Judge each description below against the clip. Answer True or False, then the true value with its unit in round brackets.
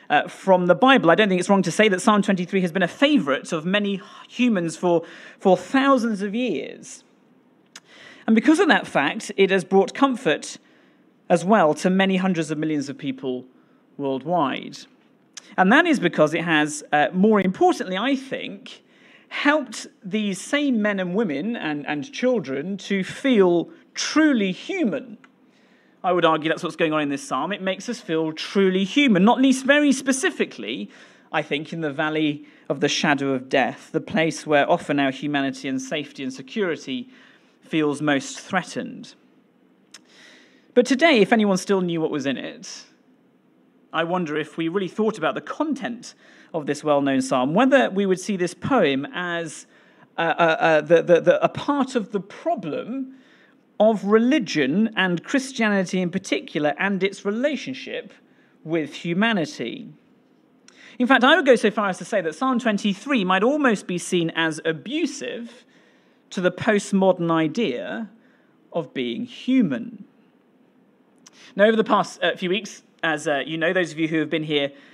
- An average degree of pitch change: False (7.2 semitones)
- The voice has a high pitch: True (195 Hz)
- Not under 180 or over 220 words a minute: False (165 wpm)